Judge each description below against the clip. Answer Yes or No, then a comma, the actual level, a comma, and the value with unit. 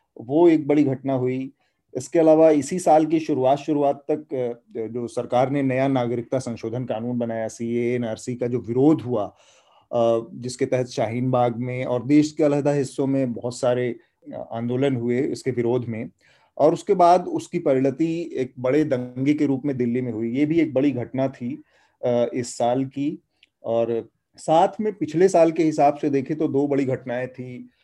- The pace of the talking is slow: No, average, 175 wpm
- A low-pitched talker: Yes, low, 130 Hz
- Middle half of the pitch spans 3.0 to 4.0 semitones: Yes, average, 3.5 semitones